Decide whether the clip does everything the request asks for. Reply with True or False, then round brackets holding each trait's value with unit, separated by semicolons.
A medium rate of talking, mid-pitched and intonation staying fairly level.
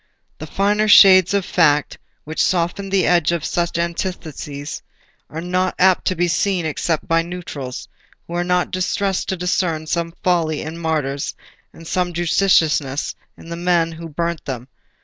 True (160 wpm; 170 Hz; 2.3 semitones)